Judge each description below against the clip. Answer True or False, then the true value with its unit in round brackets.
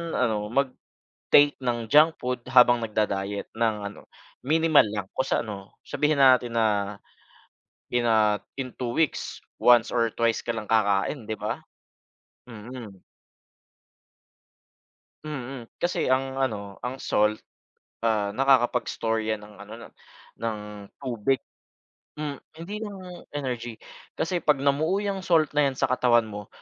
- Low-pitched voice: True (120 Hz)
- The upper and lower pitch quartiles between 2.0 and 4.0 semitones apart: False (4.4 semitones)